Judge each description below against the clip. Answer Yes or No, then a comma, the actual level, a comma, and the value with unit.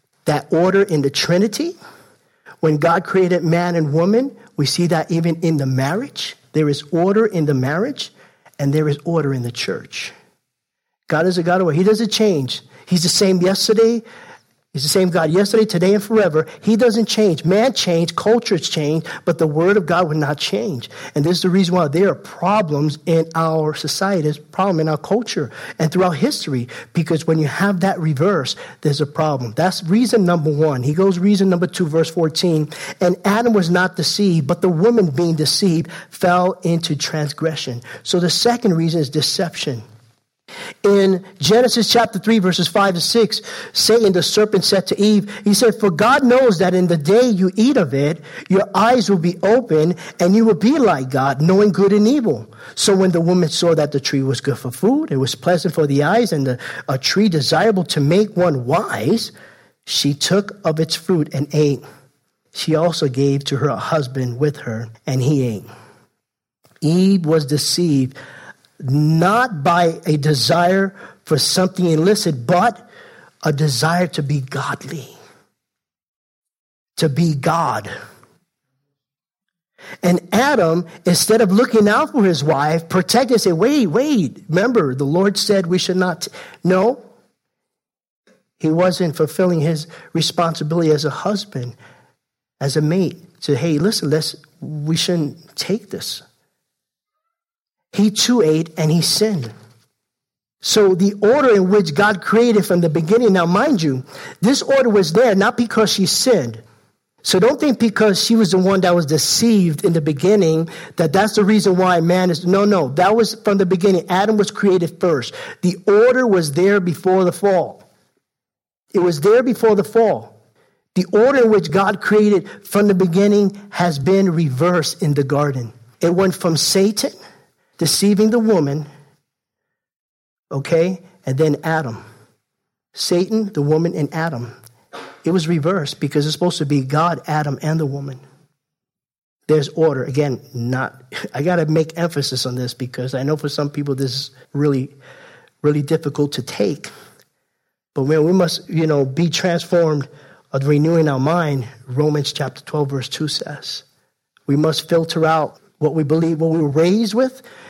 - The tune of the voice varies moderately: Yes, average, 4.8 semitones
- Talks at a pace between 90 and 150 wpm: No, average, 170 wpm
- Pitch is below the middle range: No, medium, 170 Hz